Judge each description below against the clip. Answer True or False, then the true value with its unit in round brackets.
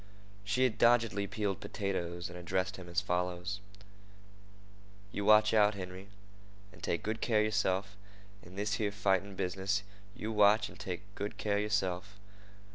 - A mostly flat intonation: True (2.2 semitones)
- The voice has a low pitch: True (100 Hz)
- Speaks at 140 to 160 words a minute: True (150 wpm)